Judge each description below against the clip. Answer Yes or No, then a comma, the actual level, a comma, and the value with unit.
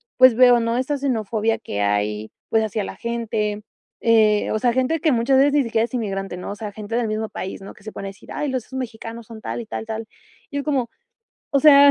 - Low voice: No, high, 230 Hz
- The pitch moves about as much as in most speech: Yes, average, 3.2 semitones